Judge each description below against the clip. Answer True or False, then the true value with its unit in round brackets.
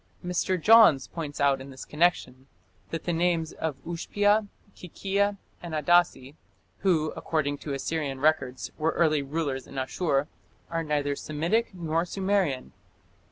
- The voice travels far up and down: False (3.8 semitones)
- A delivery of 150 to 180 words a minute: False (135 wpm)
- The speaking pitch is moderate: True (160 Hz)